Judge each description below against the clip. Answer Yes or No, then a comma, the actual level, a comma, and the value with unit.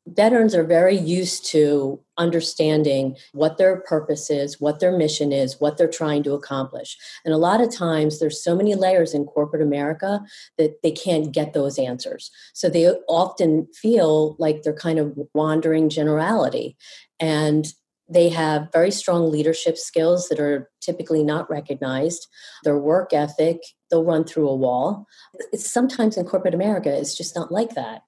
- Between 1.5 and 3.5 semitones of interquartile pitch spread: Yes, average, 2.7 semitones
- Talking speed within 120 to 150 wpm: No, average, 165 wpm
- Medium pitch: Yes, medium, 160 Hz